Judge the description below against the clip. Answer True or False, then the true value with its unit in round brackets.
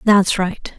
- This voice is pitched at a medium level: False (195 Hz)